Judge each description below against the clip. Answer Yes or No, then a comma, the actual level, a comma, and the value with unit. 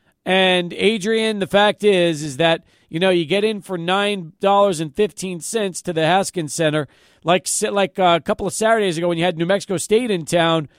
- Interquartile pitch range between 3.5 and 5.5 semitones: No, average, 3.0 semitones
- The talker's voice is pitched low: No, medium, 185 Hz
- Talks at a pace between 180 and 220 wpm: Yes, fast, 205 wpm